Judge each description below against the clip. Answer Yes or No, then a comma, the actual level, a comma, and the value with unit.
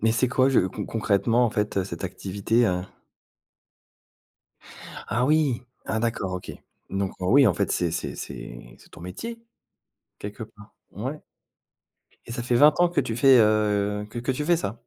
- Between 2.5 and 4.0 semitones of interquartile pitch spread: No, average, 4.4 semitones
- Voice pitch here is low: Yes, low, 110 Hz